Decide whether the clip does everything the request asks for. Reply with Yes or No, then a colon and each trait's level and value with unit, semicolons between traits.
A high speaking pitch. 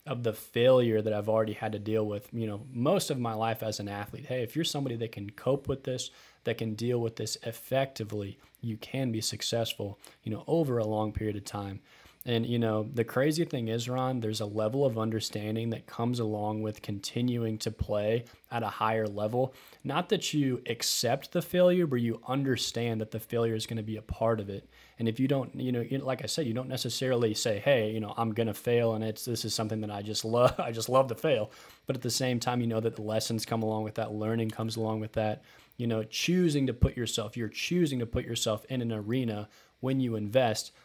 No: low, 115 Hz